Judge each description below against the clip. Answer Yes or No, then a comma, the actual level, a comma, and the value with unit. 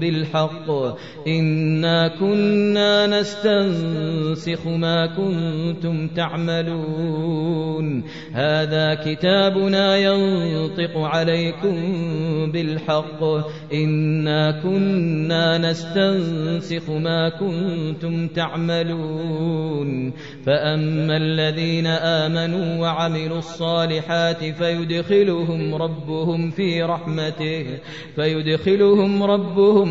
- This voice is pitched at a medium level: Yes, medium, 165 Hz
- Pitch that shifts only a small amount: Yes, narrow, 1.4 semitones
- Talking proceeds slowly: Yes, slow, 60 wpm